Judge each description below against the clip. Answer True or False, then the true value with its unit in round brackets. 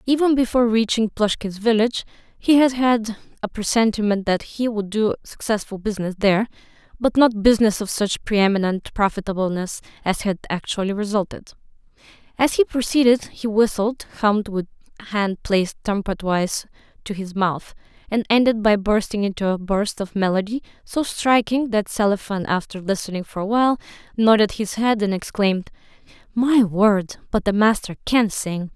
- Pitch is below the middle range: False (210 Hz)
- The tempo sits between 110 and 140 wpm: False (150 wpm)